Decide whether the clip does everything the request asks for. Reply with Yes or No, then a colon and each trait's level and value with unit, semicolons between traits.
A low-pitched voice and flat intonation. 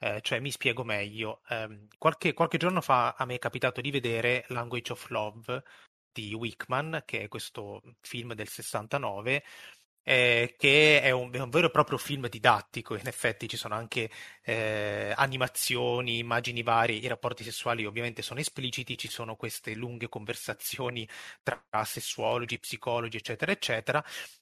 Yes: low, 120 Hz; narrow, 2.1 semitones